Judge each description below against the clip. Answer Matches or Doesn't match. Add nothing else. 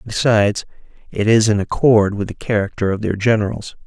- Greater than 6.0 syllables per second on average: Doesn't match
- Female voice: Doesn't match